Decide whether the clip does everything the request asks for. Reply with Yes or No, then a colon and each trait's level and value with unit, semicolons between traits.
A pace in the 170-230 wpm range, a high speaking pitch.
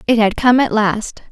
Yes: fast, 225 wpm; high, 225 Hz